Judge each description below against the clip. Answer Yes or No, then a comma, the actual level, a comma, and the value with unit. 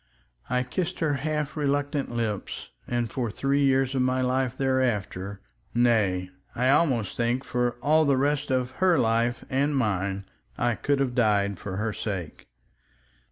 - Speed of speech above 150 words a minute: No, average, 145 wpm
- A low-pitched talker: Yes, low, 125 Hz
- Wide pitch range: No, average, 3.9 semitones